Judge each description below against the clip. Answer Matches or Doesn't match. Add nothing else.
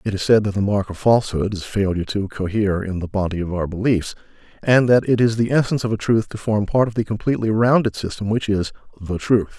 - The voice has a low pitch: Matches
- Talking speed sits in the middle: Doesn't match